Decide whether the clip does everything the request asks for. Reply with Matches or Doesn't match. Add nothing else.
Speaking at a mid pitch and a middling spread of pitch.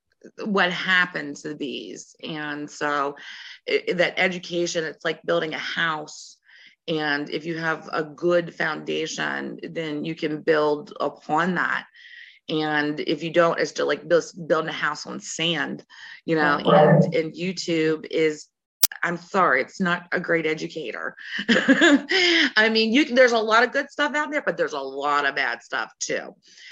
Doesn't match